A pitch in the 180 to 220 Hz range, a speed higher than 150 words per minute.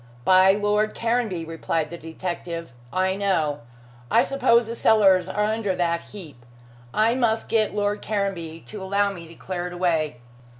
Yes: high, 190 Hz; average, 160 wpm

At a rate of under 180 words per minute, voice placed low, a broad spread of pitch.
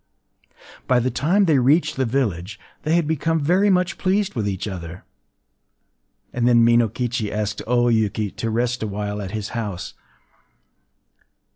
Yes: average, 150 wpm; low, 120 Hz; wide, 5.7 semitones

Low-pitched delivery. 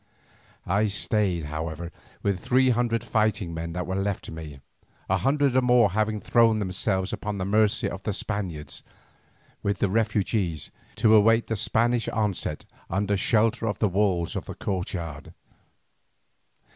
Yes: low, 100 Hz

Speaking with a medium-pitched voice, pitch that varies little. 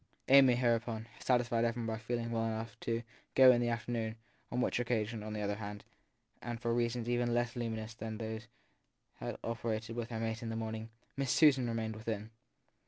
No: low, 115 Hz; narrow, 1.3 semitones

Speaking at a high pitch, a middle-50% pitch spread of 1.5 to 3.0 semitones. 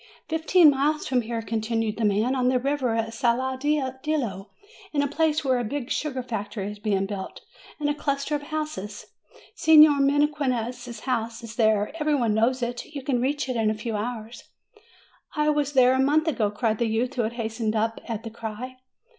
No: high, 245 Hz; average, 4.3 semitones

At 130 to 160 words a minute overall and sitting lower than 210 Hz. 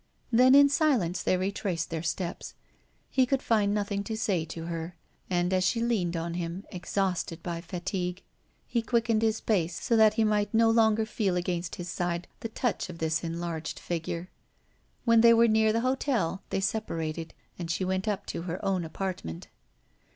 No: average, 180 wpm; high, 190 Hz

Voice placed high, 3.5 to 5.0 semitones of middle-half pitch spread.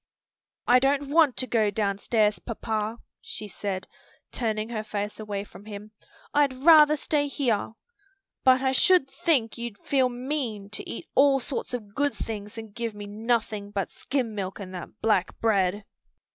Yes: high, 225 Hz; average, 4.2 semitones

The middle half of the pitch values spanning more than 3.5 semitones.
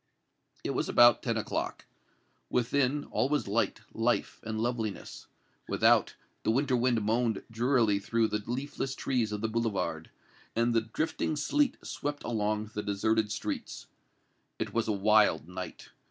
No: average, 2.7 semitones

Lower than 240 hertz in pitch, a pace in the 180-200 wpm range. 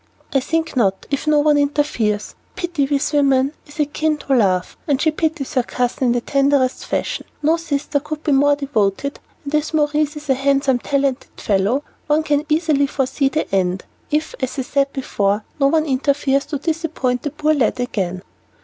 No: very high, 280 Hz; average, 185 wpm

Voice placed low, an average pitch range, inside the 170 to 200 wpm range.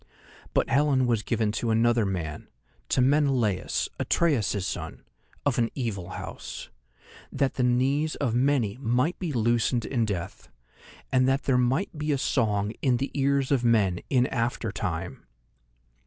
No: low, 120 Hz; average, 3.9 semitones; average, 150 wpm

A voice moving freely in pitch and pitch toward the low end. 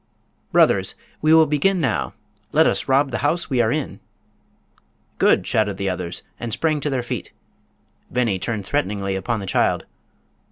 Yes: wide, 7.1 semitones; low, 120 Hz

